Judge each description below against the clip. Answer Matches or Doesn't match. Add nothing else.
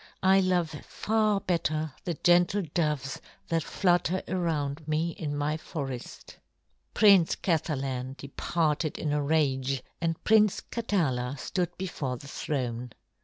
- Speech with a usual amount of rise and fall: Matches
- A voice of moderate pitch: Matches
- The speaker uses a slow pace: Matches